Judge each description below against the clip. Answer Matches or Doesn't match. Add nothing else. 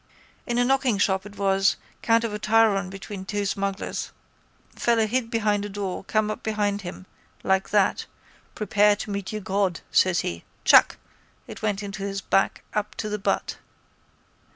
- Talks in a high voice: Matches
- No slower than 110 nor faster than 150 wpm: Doesn't match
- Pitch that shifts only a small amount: Matches